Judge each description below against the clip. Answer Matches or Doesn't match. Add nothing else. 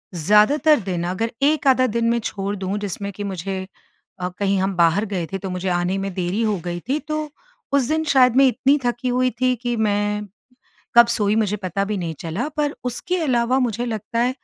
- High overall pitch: Matches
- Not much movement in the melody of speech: Doesn't match